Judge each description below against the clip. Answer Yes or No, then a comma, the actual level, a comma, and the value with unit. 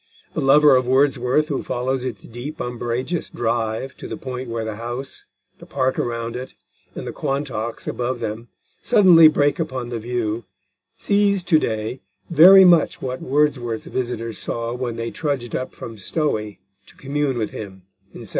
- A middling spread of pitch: Yes, average, 3.7 semitones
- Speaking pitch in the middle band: No, low, 125 Hz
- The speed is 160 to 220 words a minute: Yes, average, 165 wpm